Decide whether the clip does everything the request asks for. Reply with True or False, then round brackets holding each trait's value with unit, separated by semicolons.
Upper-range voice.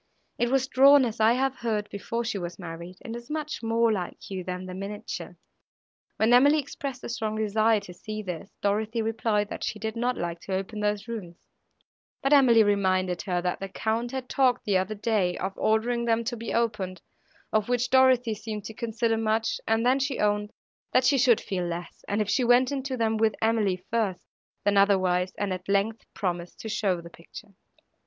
True (220 Hz)